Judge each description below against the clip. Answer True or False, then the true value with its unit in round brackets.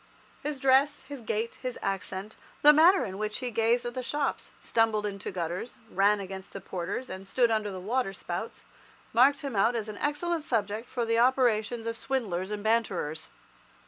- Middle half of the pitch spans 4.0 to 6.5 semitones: True (4.3 semitones)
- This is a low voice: False (225 Hz)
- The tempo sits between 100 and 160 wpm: False (175 wpm)